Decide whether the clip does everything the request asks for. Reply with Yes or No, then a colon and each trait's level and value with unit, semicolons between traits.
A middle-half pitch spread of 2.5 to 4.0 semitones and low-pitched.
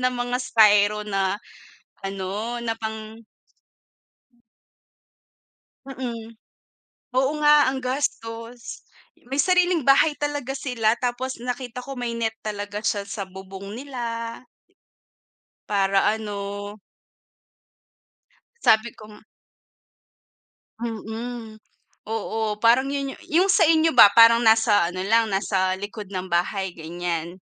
No: average, 3.6 semitones; high, 225 Hz